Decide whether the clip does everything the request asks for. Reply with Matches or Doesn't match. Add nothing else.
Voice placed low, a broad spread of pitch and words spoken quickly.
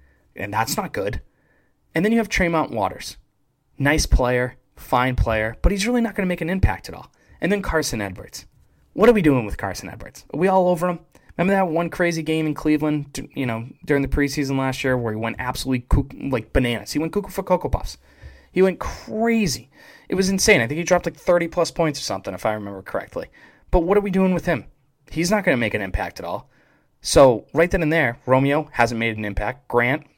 Doesn't match